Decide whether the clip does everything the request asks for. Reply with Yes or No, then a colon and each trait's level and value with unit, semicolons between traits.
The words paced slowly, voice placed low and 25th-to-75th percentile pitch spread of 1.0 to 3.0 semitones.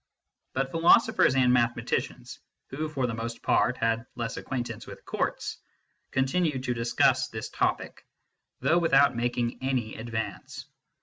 Yes: slow, 130 wpm; low, 125 Hz; narrow, 2.6 semitones